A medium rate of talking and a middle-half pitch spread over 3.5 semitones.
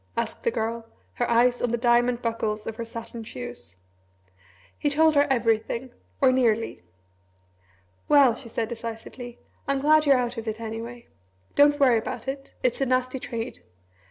No: average, 160 wpm; narrow, 2.4 semitones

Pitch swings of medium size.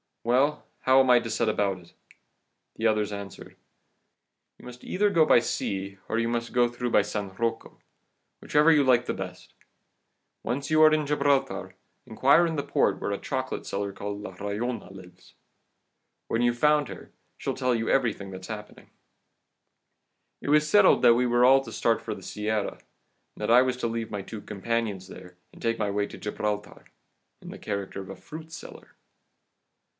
Yes: average, 4.2 semitones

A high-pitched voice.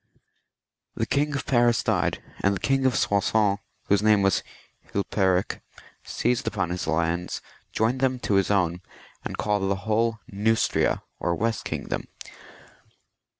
No: low, 105 Hz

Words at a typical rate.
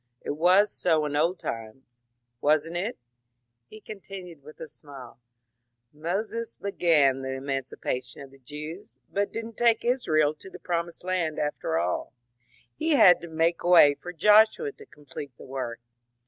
Yes: average, 170 wpm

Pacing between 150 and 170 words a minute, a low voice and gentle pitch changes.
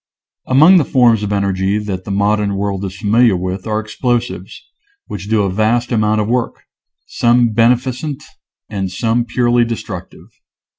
No: average, 155 wpm; low, 110 Hz; average, 3.2 semitones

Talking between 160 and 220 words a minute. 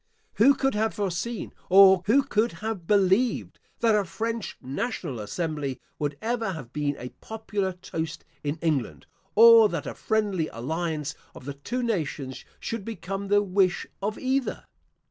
No: average, 150 wpm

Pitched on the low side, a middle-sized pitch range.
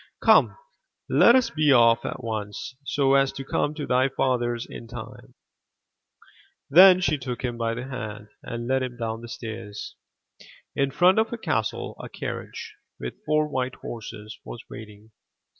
Yes: low, 125 Hz; average, 3.3 semitones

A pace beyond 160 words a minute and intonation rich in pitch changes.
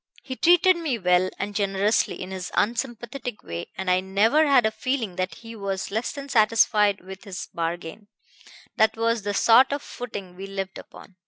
No: average, 180 wpm; average, 3.9 semitones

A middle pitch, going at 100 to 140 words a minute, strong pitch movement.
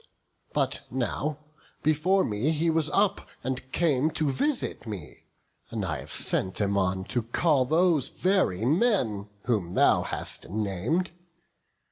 No: low, 130 Hz; slow, 135 wpm; wide, 7.8 semitones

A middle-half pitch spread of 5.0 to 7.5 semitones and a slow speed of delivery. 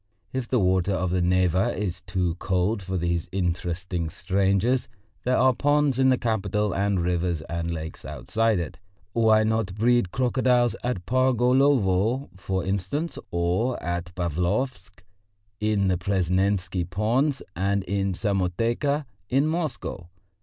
Yes: average, 5.3 semitones; slow, 130 wpm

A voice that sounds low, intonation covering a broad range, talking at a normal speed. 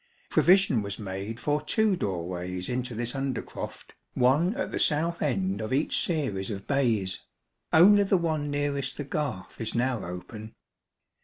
Yes: low, 130 Hz; wide, 7.0 semitones; average, 155 wpm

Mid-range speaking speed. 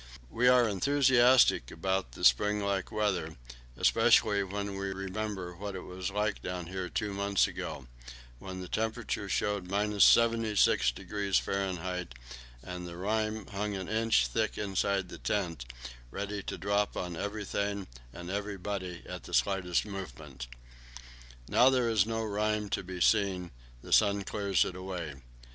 Yes: average, 145 wpm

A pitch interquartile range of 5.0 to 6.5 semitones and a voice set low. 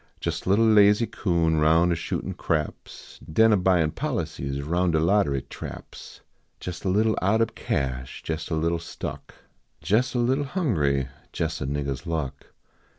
Yes: wide, 5.5 semitones; very low, 85 Hz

